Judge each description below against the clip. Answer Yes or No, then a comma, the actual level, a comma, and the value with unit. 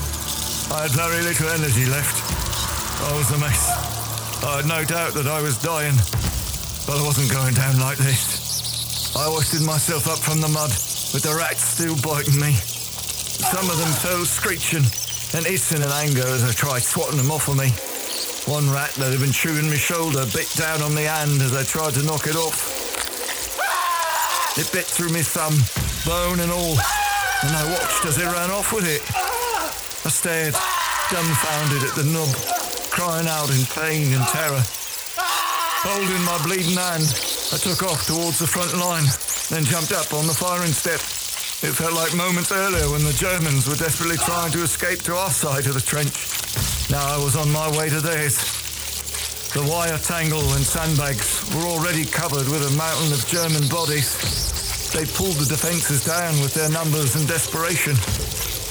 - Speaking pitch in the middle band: Yes, medium, 150 Hz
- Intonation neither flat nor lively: Yes, average, 3.7 semitones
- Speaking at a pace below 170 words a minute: No, average, 175 wpm